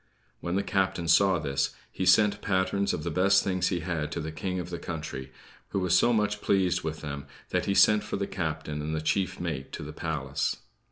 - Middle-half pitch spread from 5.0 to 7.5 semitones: No, average, 3.9 semitones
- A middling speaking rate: No, fast, 220 wpm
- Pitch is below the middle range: Yes, very low, 90 Hz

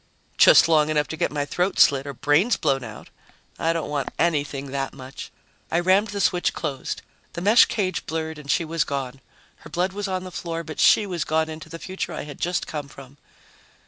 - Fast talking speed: Yes, fast, 210 wpm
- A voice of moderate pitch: Yes, medium, 160 Hz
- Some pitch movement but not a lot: Yes, average, 3.7 semitones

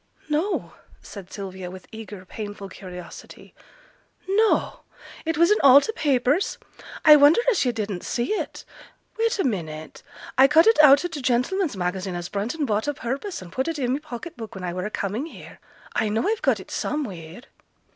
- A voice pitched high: Yes, high, 245 Hz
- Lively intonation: Yes, wide, 8.0 semitones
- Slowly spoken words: No, average, 185 wpm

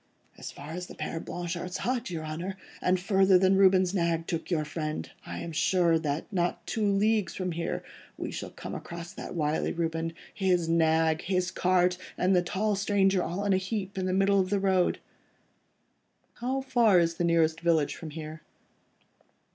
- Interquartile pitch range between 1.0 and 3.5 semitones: Yes, average, 2.7 semitones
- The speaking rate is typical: Yes, average, 180 wpm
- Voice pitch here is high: No, medium, 180 Hz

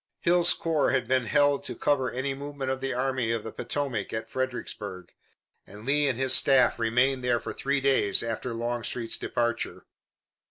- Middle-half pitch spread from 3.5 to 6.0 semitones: No, average, 2.9 semitones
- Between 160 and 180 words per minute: Yes, average, 170 wpm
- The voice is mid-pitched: No, low, 130 Hz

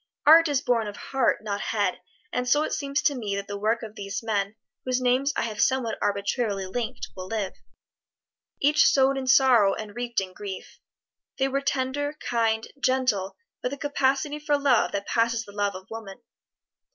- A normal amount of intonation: Yes, average, 4.7 semitones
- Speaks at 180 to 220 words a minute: Yes, average, 185 wpm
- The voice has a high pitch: Yes, high, 235 Hz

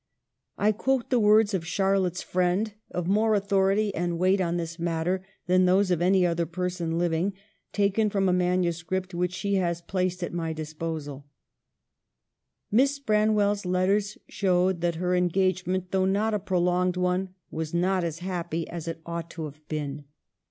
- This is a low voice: No, medium, 180 Hz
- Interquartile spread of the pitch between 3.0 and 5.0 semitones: No, narrow, 2.5 semitones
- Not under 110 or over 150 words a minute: No, average, 165 wpm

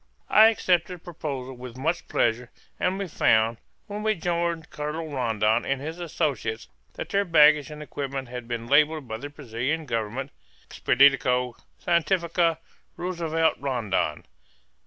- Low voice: No, medium, 145 Hz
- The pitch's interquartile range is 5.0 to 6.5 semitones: Yes, average, 5.3 semitones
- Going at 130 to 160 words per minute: Yes, slow, 135 wpm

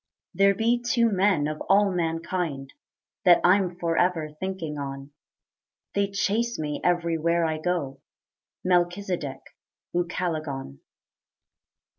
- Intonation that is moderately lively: Yes, average, 3.8 semitones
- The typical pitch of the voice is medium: Yes, medium, 175 Hz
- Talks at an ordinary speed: No, slow, 100 wpm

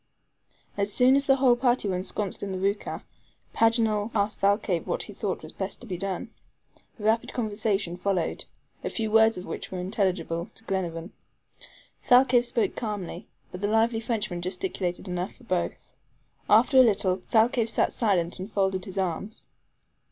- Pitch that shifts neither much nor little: Yes, average, 3.5 semitones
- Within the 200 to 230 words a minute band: No, average, 165 wpm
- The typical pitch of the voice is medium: No, high, 205 Hz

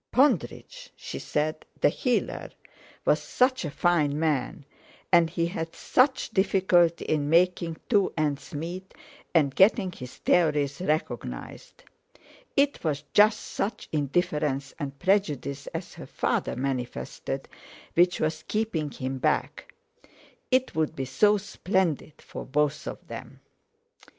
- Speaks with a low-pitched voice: No, medium, 165 Hz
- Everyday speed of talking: No, slow, 120 wpm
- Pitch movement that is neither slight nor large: Yes, average, 4.7 semitones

